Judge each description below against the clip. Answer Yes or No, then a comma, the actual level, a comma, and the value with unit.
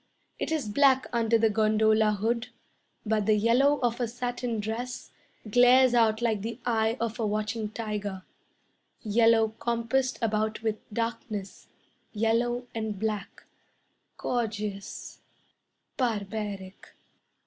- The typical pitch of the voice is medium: No, high, 225 Hz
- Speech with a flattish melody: Yes, narrow, 2.0 semitones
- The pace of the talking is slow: Yes, slow, 115 wpm